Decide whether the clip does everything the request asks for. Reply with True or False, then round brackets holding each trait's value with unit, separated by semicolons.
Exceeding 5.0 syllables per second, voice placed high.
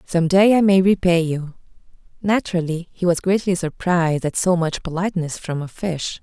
False (5.2 syllables/s; 175 Hz)